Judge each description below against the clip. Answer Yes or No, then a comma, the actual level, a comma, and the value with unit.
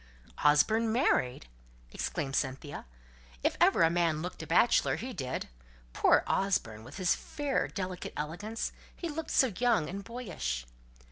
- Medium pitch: Yes, medium, 180 Hz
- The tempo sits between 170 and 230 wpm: No, average, 140 wpm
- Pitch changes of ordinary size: No, wide, 7.7 semitones